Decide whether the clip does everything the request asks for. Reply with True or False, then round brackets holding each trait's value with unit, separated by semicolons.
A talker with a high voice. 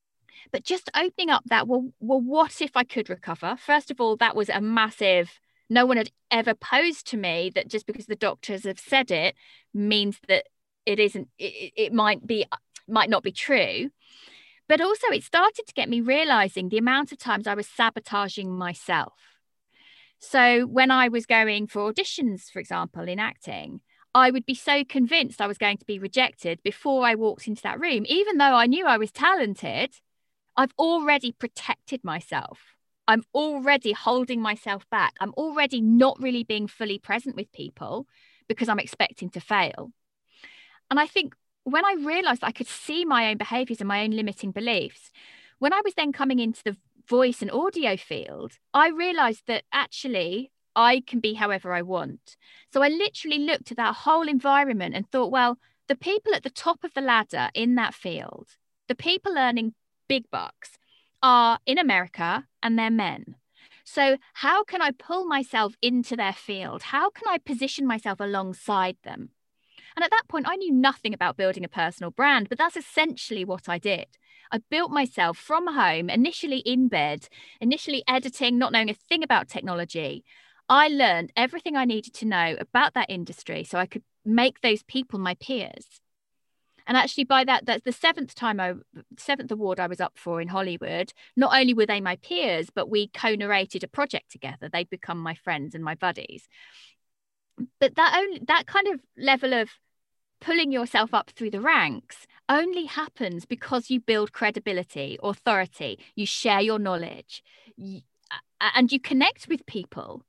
True (240 Hz)